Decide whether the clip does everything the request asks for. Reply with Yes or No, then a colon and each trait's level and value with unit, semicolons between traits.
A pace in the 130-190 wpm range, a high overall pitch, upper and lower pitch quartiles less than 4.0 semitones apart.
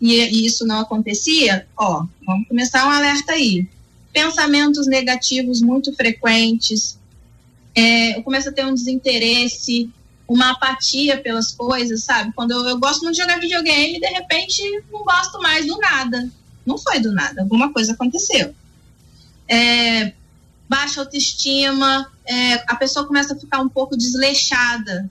Yes: average, 145 wpm; very high, 255 Hz; average, 3.4 semitones